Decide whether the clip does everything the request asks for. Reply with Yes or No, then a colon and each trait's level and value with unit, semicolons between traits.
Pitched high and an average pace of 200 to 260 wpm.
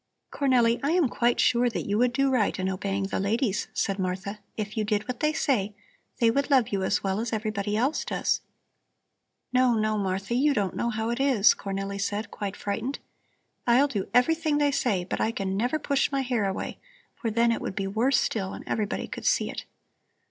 Yes: high, 225 Hz; fast, 205 wpm